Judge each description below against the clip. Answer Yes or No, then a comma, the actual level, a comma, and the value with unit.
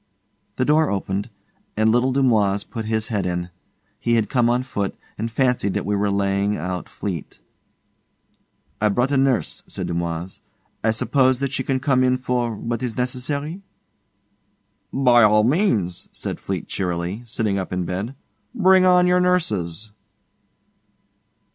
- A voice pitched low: Yes, low, 115 Hz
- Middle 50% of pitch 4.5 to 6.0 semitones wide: Yes, average, 4.8 semitones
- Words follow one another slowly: No, average, 150 wpm